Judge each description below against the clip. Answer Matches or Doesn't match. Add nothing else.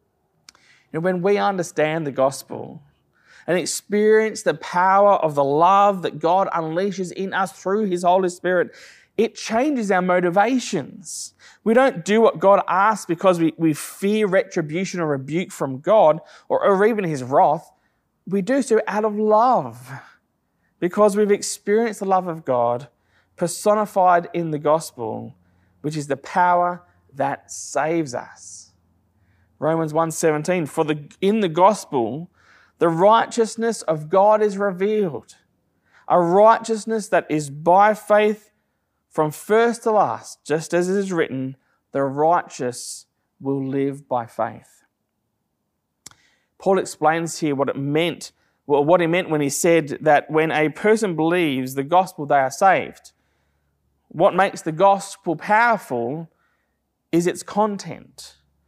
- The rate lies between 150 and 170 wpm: Doesn't match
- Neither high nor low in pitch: Matches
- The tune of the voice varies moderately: Doesn't match